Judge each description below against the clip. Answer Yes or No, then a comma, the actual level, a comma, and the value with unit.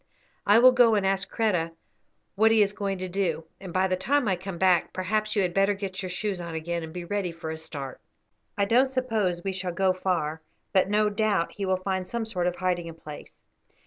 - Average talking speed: No, fast, 225 wpm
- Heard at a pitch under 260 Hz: Yes, high, 190 Hz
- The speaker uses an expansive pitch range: No, average, 2.9 semitones